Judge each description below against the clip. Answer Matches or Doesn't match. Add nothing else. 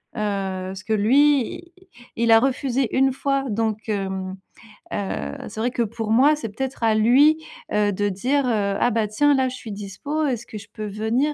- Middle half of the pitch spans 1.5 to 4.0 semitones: Doesn't match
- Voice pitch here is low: Doesn't match